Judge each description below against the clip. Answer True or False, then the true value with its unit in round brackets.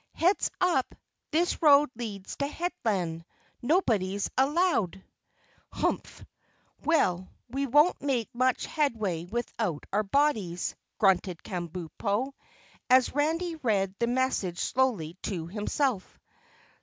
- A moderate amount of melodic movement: False (7.4 semitones)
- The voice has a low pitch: False (235 Hz)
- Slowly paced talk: True (105 wpm)